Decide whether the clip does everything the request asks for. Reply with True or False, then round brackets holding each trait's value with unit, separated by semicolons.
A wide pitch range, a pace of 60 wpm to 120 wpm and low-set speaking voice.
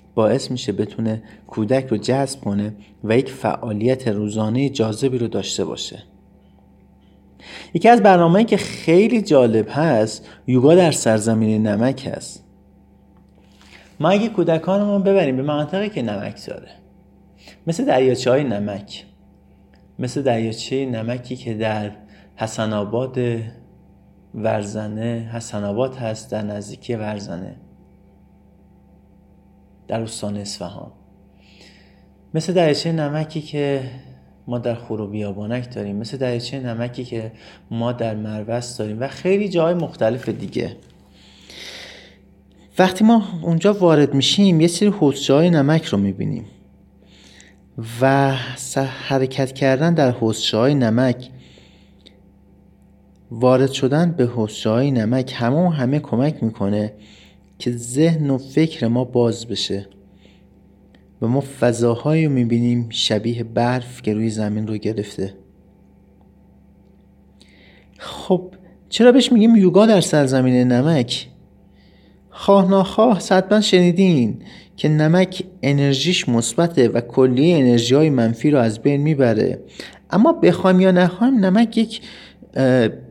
True (6.0 semitones; 115 wpm; 120 Hz)